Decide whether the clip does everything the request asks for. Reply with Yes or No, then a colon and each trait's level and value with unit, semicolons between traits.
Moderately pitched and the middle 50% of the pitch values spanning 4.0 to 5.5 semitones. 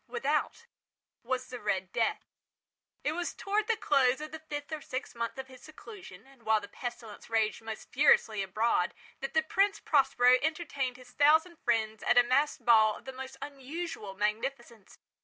No: very high, 255 Hz; average, 5.0 semitones